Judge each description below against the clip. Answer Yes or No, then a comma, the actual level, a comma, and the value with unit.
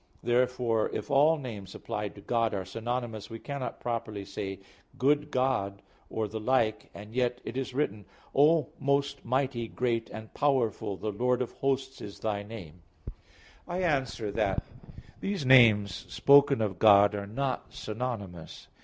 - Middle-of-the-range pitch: No, low, 115 Hz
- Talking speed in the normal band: Yes, average, 155 wpm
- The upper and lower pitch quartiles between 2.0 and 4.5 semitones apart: Yes, average, 4.2 semitones